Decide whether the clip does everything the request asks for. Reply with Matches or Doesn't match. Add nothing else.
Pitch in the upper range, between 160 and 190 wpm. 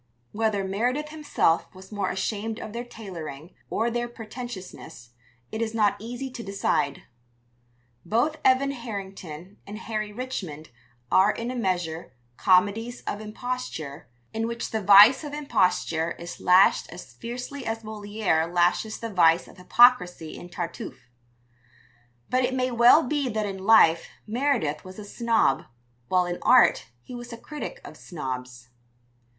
Doesn't match